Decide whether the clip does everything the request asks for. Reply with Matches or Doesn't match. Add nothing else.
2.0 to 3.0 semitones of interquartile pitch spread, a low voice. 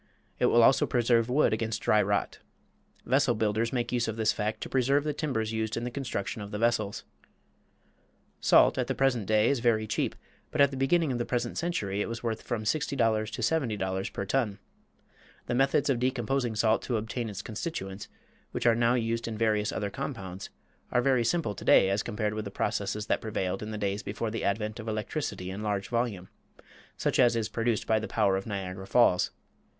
Matches